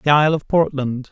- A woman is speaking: No, male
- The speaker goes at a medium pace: No, fast, 215 wpm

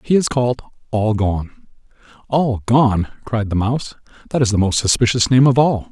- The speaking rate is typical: Yes, average, 180 wpm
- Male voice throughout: Yes, male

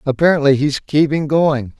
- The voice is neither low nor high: Yes, medium, 145 Hz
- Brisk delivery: No, slow, 135 wpm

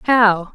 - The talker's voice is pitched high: Yes, high, 210 Hz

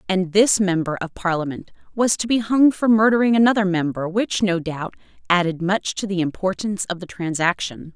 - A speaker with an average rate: Yes, average, 180 wpm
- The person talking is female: Yes, female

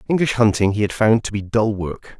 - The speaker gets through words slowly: No, fast, 245 wpm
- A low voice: Yes, low, 110 Hz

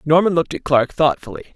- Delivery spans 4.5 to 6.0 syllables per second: No, 6.5 syllables/s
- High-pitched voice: No, medium, 155 Hz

